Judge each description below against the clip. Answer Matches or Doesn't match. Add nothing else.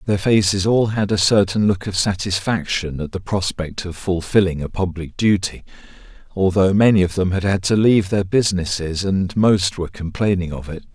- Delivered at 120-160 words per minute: Doesn't match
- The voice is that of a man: Matches